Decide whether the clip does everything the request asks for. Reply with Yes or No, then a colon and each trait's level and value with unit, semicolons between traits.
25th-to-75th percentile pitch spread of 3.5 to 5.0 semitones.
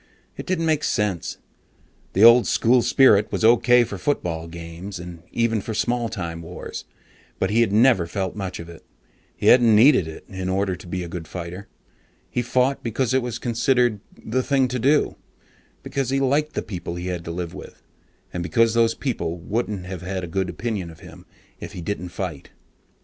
No: wide, 5.5 semitones